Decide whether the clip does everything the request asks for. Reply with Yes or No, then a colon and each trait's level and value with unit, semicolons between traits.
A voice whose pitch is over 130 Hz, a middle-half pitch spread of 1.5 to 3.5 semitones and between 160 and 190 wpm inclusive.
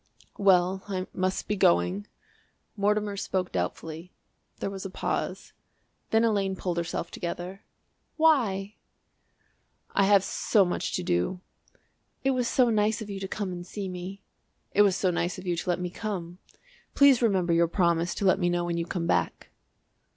Yes: medium, 185 Hz; average, 2.7 semitones; average, 170 wpm